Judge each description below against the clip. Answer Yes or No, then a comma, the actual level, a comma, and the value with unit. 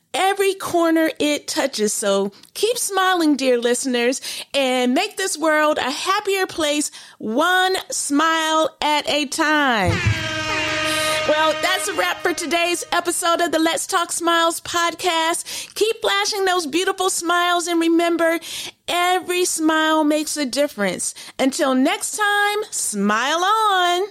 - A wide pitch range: No, average, 3.9 semitones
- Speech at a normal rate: No, slow, 125 wpm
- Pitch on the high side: Yes, very high, 330 Hz